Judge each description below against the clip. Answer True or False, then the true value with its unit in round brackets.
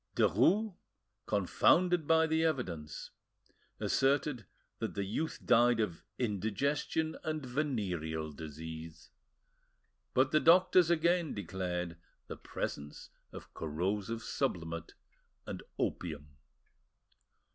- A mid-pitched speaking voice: False (110 Hz)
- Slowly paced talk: True (90 wpm)